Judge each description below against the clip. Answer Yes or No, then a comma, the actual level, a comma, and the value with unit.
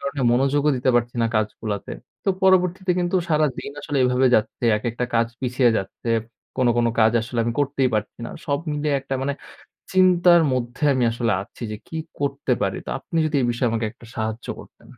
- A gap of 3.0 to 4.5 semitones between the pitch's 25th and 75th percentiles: Yes, average, 3.9 semitones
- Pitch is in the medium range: No, low, 130 Hz